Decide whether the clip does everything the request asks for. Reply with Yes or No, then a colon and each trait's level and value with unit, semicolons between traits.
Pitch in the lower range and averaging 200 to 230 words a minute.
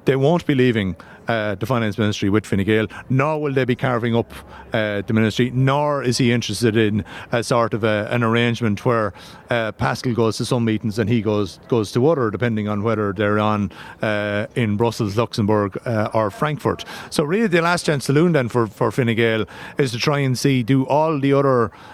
Yes: low, 115 Hz; fast, 205 wpm